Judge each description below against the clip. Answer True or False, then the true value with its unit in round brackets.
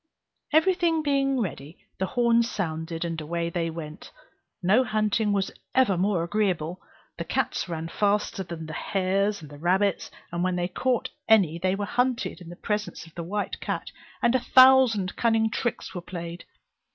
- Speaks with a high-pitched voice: True (195 Hz)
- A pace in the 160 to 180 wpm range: True (170 wpm)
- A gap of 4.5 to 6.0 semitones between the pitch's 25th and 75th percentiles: True (4.9 semitones)